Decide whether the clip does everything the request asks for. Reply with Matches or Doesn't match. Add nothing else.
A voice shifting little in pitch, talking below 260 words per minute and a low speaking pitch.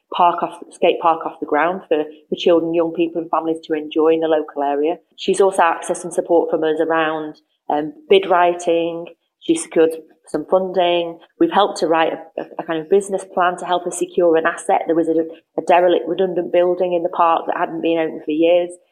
Doesn't match